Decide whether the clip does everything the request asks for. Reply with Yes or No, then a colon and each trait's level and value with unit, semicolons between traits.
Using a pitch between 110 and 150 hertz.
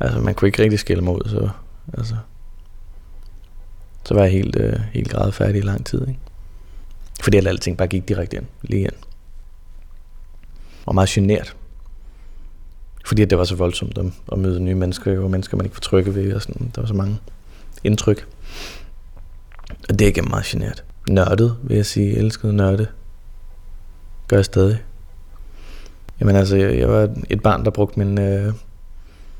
No: very low, 95 Hz